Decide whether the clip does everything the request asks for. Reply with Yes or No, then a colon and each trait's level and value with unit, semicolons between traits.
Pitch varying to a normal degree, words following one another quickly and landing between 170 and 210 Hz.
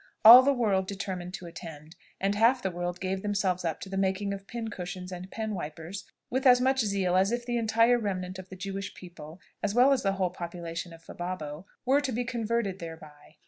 Yes: average, 4.2 semitones; fast, 210 wpm; high, 190 Hz